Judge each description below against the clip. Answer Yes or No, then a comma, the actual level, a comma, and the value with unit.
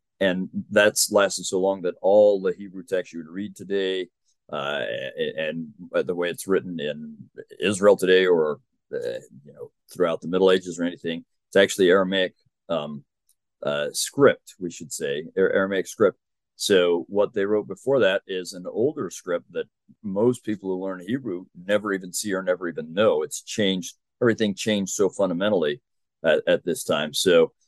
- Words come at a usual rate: Yes, average, 175 wpm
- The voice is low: Yes, low, 100 Hz